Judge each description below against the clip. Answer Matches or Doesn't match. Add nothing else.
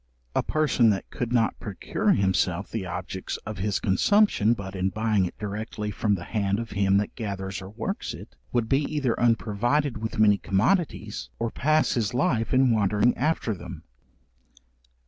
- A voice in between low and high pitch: Doesn't match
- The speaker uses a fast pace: Doesn't match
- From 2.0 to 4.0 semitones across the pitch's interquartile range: Matches